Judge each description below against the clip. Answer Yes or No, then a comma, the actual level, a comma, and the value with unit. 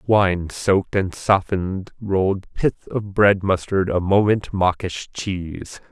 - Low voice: Yes, very low, 95 Hz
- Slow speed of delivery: Yes, slow, 130 wpm